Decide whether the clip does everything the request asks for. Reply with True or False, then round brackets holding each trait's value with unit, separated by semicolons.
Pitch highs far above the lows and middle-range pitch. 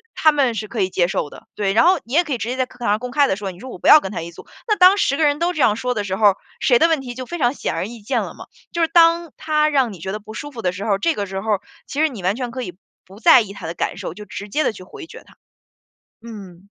False (7.0 semitones; 235 Hz)